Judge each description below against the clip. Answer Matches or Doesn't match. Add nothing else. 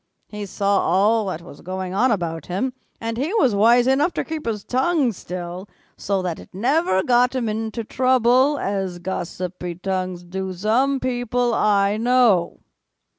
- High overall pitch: Matches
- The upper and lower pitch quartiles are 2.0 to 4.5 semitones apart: Doesn't match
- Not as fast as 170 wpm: Matches